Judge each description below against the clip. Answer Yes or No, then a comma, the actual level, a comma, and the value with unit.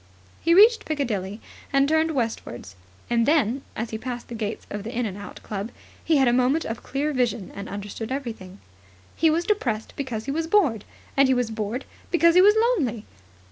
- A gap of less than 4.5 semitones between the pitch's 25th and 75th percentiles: No, wide, 5.6 semitones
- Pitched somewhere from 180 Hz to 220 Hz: No, high, 245 Hz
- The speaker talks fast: No, average, 195 wpm